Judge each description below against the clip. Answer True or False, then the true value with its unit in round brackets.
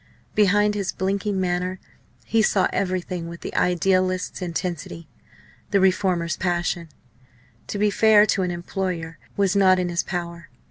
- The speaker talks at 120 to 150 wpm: True (140 wpm)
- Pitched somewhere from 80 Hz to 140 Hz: False (185 Hz)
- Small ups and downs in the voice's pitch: True (2.2 semitones)